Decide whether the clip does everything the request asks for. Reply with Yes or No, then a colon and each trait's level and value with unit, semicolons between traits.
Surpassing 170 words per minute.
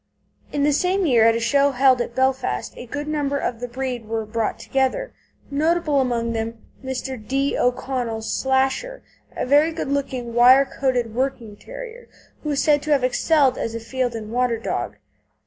Yes: average, 180 wpm